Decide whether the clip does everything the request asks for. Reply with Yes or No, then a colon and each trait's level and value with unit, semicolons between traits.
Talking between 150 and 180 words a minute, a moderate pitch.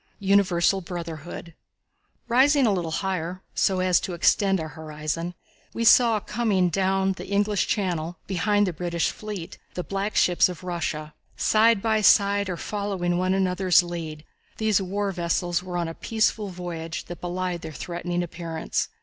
Yes: average, 155 wpm; medium, 180 Hz